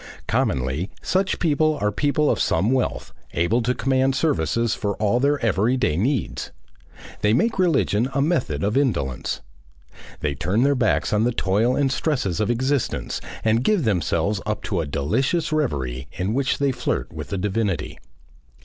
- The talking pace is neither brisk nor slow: Yes, average, 160 wpm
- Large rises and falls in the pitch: Yes, wide, 6.5 semitones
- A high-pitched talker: No, low, 115 Hz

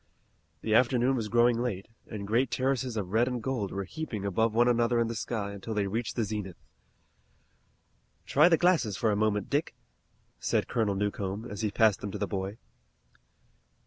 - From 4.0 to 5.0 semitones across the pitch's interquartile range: No, average, 3.0 semitones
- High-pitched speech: No, low, 110 Hz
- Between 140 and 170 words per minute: No, average, 180 wpm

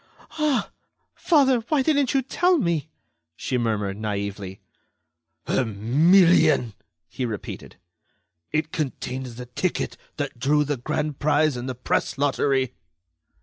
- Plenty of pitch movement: Yes, wide, 6.3 semitones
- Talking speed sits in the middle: No, slow, 120 wpm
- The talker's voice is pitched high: No, medium, 140 Hz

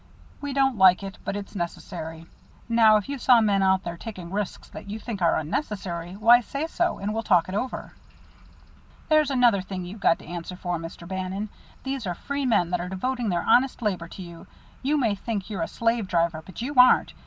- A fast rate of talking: Yes, fast, 210 wpm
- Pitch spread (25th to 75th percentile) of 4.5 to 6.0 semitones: Yes, average, 5.1 semitones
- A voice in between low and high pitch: No, high, 200 Hz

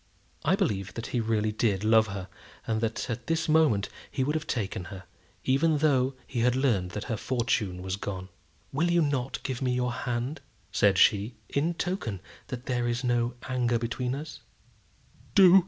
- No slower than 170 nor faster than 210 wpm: Yes, average, 175 wpm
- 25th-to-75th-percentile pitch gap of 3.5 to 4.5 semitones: Yes, average, 3.8 semitones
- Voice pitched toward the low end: Yes, low, 120 Hz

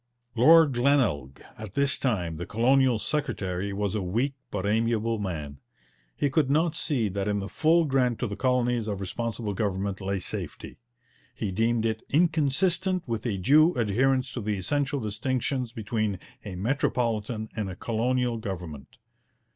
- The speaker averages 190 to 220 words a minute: No, average, 155 wpm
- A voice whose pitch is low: Yes, low, 115 Hz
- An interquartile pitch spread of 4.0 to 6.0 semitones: Yes, average, 4.9 semitones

